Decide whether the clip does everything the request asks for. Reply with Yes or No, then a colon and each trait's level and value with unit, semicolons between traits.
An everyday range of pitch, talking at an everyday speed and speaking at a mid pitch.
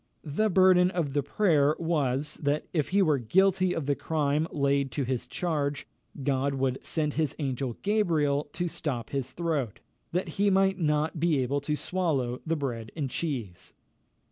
Yes: average, 4.0 semitones; average, 170 wpm; medium, 150 Hz